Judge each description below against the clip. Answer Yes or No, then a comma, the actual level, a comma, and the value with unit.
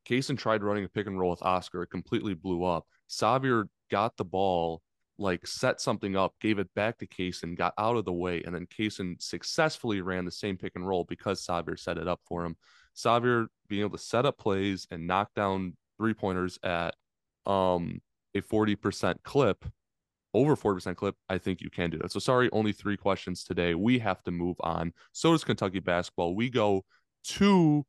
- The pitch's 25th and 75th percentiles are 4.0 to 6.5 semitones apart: No, average, 3.3 semitones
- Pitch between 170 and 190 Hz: No, very low, 95 Hz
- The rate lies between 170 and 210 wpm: Yes, average, 200 wpm